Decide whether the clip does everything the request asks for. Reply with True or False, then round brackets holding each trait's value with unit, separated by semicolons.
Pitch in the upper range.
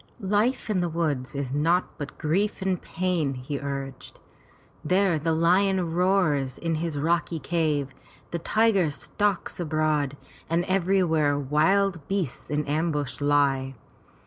False (160 Hz)